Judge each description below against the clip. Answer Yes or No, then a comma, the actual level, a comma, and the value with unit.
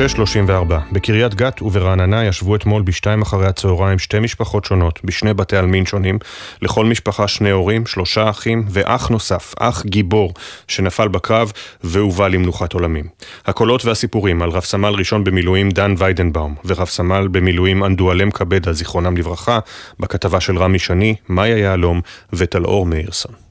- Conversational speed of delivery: Yes, average, 140 wpm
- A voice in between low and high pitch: No, low, 100 Hz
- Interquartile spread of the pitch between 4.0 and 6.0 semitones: No, narrow, 2.6 semitones